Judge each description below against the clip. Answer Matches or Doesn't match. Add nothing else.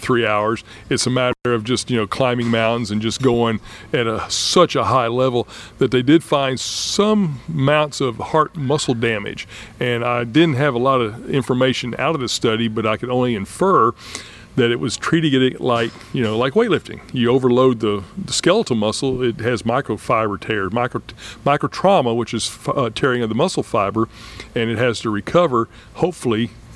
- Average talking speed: Matches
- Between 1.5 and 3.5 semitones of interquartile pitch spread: Matches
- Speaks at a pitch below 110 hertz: Doesn't match